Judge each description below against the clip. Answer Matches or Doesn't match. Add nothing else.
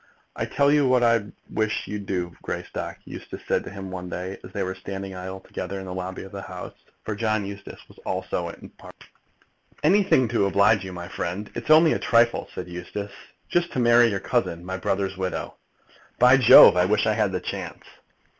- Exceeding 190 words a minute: Matches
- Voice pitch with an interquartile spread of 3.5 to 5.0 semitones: Matches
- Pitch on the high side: Doesn't match